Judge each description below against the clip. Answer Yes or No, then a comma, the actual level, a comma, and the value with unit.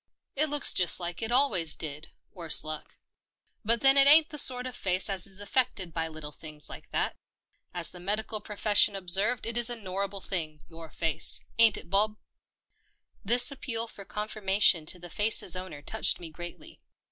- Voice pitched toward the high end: Yes, high, 195 Hz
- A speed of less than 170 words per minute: No, average, 195 wpm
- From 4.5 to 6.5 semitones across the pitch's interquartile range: Yes, average, 5.1 semitones